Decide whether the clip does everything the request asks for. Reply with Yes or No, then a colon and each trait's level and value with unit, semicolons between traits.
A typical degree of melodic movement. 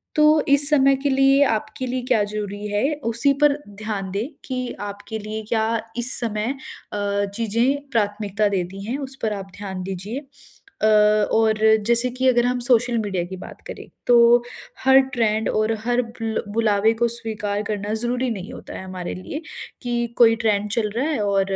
Yes: average, 3.2 semitones